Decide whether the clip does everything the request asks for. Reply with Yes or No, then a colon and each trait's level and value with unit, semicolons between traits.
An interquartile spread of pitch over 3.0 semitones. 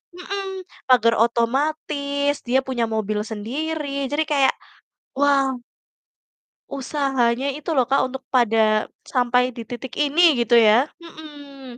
Yes: average, 3.5 semitones